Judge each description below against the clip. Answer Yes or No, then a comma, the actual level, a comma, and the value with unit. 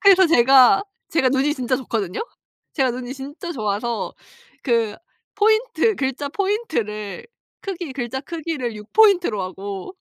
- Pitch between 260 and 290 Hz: Yes, very high, 265 Hz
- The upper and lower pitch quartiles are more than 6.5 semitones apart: Yes, wide, 7.0 semitones